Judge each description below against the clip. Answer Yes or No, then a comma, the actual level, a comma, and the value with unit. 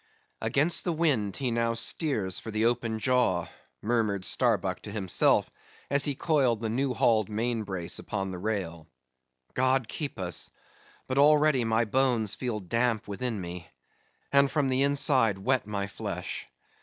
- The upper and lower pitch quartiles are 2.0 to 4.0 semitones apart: No, average, 4.6 semitones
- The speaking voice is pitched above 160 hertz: No, low, 115 Hz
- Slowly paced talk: No, average, 155 wpm